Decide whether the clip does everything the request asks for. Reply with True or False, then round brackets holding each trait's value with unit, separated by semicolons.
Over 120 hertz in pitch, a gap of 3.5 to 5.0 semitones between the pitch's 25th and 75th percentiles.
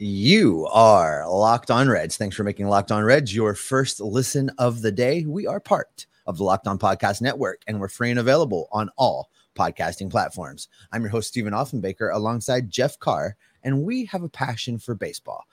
False (115 Hz; 4.1 semitones)